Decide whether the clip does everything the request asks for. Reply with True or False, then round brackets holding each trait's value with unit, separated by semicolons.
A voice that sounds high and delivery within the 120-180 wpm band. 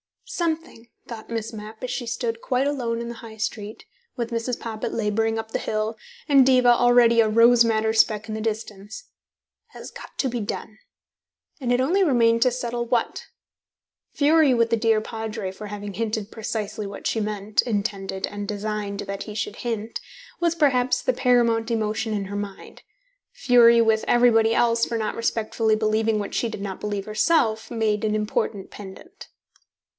True (225 Hz; 175 wpm)